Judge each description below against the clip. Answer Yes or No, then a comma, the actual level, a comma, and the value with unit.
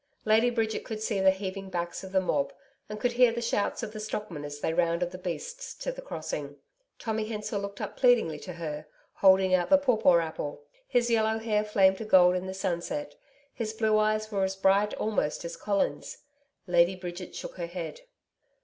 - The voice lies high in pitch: Yes, high, 195 Hz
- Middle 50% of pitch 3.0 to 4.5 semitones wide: Yes, average, 3.8 semitones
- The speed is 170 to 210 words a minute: Yes, average, 195 wpm